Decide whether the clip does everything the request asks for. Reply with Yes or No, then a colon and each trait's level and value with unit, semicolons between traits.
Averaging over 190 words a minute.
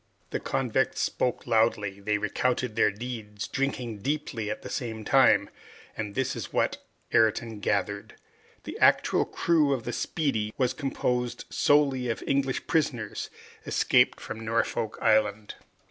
No: slow, 135 wpm